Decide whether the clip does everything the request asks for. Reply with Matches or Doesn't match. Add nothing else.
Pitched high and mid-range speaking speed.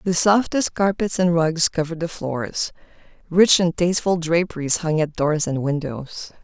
Doesn't match